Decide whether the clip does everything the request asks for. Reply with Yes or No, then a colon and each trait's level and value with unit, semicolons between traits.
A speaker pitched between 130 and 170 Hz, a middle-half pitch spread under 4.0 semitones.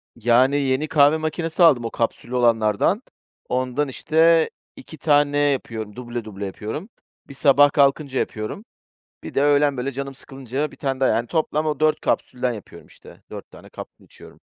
Yes: low, 135 Hz; average, 3.6 semitones